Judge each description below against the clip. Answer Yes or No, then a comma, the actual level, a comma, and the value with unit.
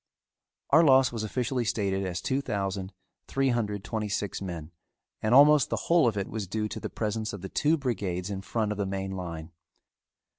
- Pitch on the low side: Yes, low, 105 Hz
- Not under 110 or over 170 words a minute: No, average, 195 wpm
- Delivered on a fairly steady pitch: No, average, 4.3 semitones